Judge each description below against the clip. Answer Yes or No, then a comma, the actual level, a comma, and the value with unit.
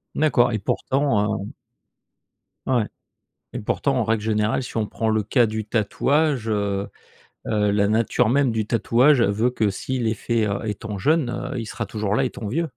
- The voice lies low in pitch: Yes, low, 110 Hz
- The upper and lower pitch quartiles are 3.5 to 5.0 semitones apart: No, average, 3.0 semitones